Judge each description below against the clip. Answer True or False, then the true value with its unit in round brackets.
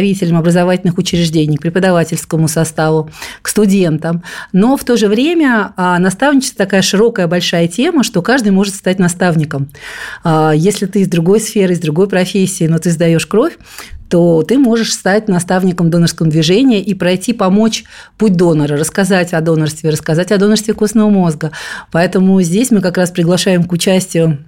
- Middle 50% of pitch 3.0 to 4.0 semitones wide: True (3.5 semitones)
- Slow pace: False (150 wpm)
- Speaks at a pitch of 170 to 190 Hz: True (185 Hz)